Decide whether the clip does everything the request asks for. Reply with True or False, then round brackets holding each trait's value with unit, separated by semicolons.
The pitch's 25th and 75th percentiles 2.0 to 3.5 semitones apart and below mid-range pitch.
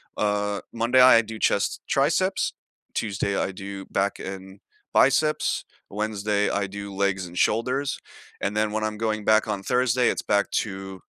True (2.7 semitones; 105 Hz)